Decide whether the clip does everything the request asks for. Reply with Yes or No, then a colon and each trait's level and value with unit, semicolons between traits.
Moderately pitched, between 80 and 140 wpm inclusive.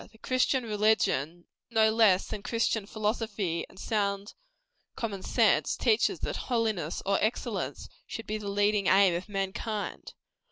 No: high, 210 Hz; slow, 135 wpm